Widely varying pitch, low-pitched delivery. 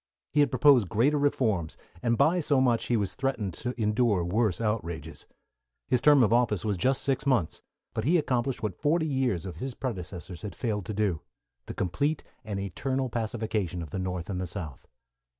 Yes: wide, 5.9 semitones; low, 110 Hz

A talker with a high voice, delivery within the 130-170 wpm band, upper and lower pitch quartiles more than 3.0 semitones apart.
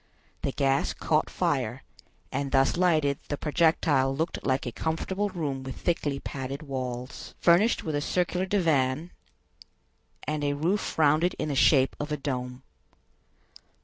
No: medium, 145 Hz; average, 145 wpm; average, 3.6 semitones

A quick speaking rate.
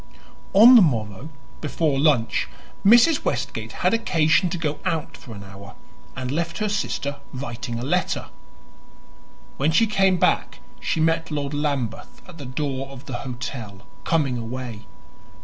No: average, 150 wpm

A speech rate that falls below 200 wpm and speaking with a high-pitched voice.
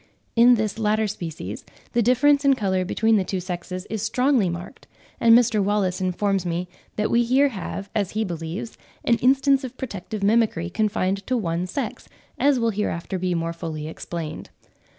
Yes: average, 170 wpm; high, 210 Hz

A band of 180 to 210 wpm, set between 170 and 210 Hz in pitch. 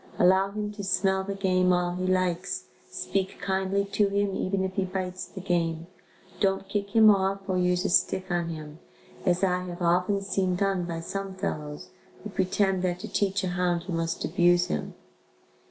Yes: average, 185 wpm; medium, 185 Hz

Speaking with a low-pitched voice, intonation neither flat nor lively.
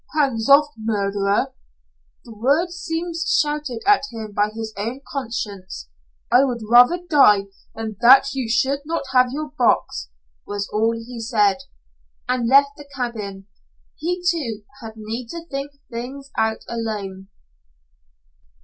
No: high, 240 Hz; average, 4.4 semitones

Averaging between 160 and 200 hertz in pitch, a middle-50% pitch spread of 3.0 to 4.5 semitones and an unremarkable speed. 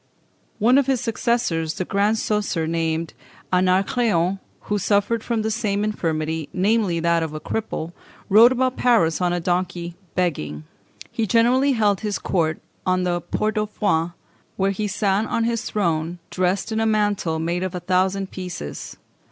Yes: high, 190 Hz; average, 4.2 semitones; average, 160 wpm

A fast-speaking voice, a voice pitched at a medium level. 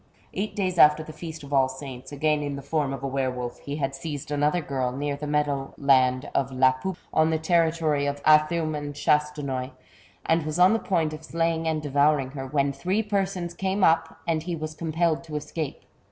Yes: fast, 210 wpm; medium, 150 Hz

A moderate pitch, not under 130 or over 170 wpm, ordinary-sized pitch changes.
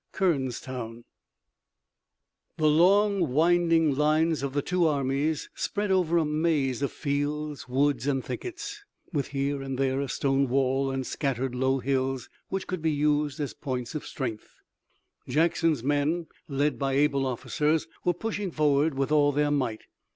Yes: medium, 145 Hz; average, 150 wpm; average, 3.1 semitones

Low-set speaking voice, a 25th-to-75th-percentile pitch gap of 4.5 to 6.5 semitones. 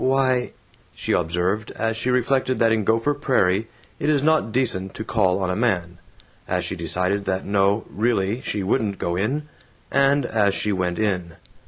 Yes: low, 110 Hz; average, 5.0 semitones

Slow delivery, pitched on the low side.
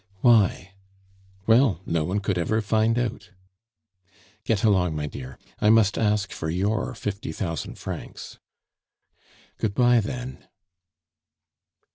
Yes: slow, 115 wpm; low, 105 Hz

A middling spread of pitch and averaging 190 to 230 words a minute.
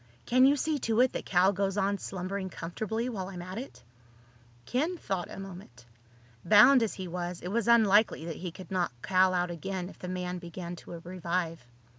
Yes: average, 3.2 semitones; average, 195 wpm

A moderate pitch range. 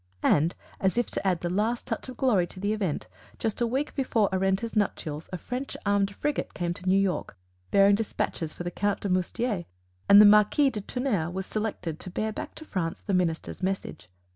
Yes: average, 3.4 semitones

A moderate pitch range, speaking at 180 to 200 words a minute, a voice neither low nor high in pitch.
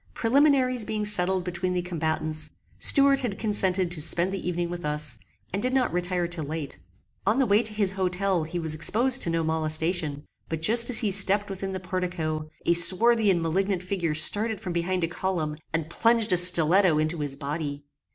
Yes: average, 4.1 semitones; average, 190 wpm; medium, 180 Hz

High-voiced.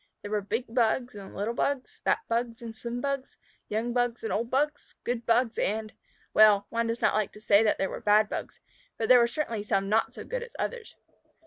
Yes: high, 230 Hz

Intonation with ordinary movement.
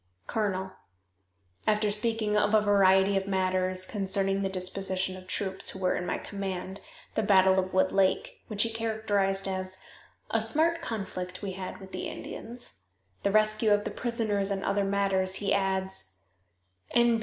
No: narrow, 2.1 semitones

